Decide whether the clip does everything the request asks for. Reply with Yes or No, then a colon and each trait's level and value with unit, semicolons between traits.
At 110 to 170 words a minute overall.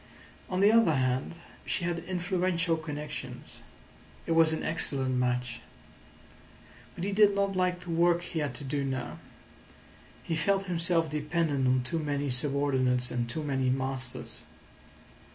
Yes: average, 145 wpm